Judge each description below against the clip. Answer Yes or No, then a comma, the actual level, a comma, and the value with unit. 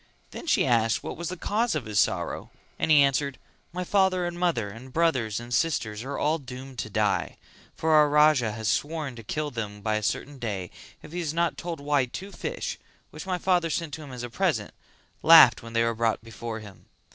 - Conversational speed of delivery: No, fast, 215 wpm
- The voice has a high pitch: No, low, 135 Hz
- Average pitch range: No, wide, 6.3 semitones